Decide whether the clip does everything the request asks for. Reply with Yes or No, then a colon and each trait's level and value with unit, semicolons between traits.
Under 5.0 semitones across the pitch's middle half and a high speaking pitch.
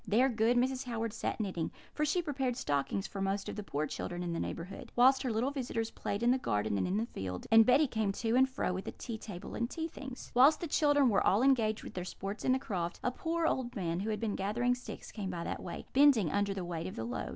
No: wide, 5.4 semitones; high, 225 Hz